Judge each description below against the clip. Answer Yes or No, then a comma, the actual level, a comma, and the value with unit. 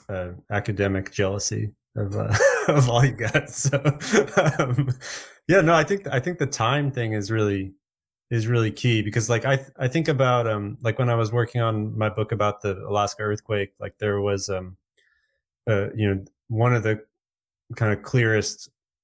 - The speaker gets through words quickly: No, average, 180 wpm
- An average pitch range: Yes, average, 4.0 semitones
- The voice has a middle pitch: No, low, 110 Hz